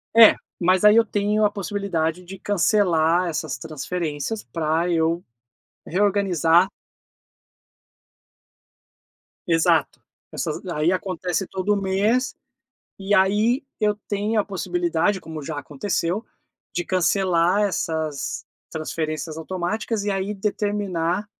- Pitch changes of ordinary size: Yes, average, 3.9 semitones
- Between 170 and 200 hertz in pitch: Yes, medium, 185 Hz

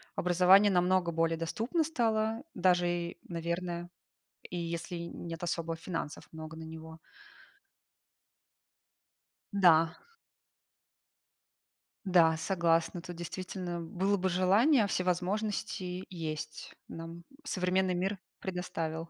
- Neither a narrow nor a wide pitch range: No, narrow, 2.2 semitones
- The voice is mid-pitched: Yes, medium, 175 Hz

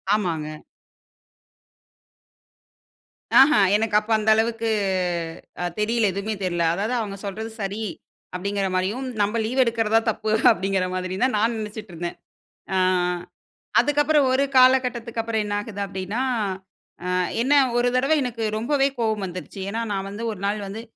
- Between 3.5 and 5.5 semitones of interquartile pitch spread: No, average, 3.0 semitones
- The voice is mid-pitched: No, high, 220 Hz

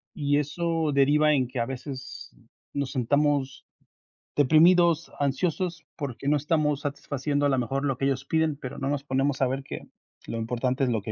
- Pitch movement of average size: No, narrow, 2.2 semitones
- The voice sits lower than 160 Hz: Yes, medium, 140 Hz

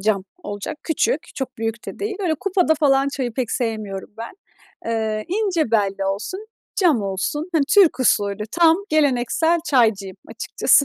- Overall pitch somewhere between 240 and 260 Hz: Yes, very high, 255 Hz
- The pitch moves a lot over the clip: Yes, wide, 7.1 semitones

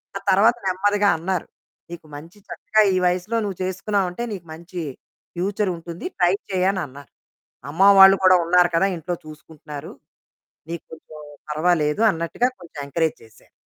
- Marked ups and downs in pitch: No, average, 2.9 semitones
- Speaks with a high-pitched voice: No, medium, 180 Hz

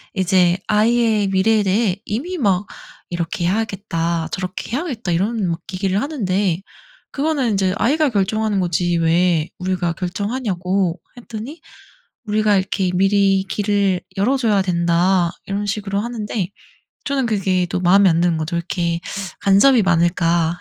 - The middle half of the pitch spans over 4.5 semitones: No, average, 3.4 semitones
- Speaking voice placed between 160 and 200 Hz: Yes, high, 195 Hz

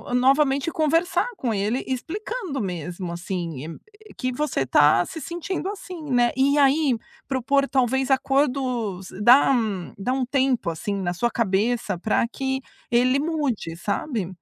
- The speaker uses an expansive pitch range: Yes, wide, 5.8 semitones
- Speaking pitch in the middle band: No, very high, 255 Hz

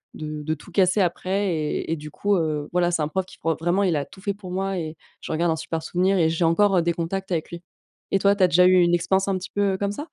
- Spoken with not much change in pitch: No, average, 3.0 semitones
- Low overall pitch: No, medium, 175 Hz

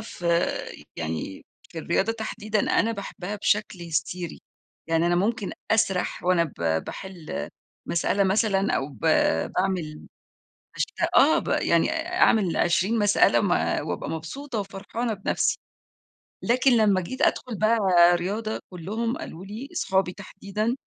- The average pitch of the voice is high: Yes, high, 195 Hz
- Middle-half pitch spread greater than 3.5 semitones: Yes, average, 4.0 semitones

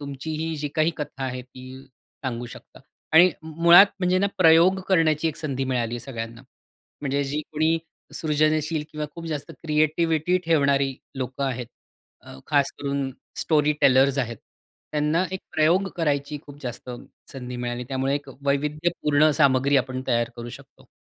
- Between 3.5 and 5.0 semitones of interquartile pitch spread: No, average, 3.1 semitones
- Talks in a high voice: No, medium, 145 Hz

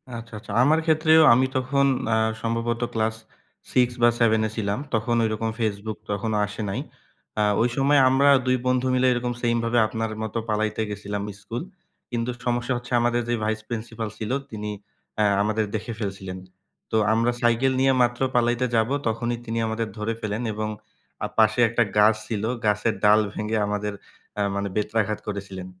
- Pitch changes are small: Yes, narrow, 2.2 semitones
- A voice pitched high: No, low, 115 Hz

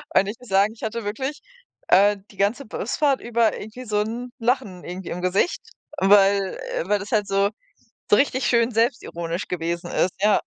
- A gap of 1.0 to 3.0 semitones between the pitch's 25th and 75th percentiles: No, average, 3.4 semitones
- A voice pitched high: Yes, high, 210 Hz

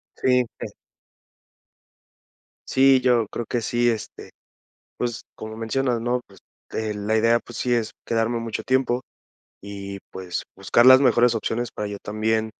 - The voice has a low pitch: Yes, low, 115 Hz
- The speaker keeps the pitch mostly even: Yes, narrow, 2.0 semitones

